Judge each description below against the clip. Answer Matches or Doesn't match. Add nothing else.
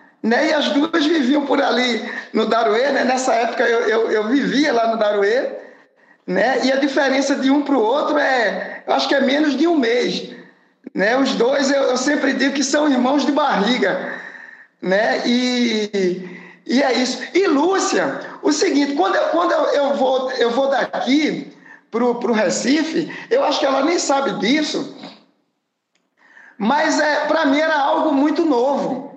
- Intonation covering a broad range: Doesn't match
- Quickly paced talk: Doesn't match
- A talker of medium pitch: Doesn't match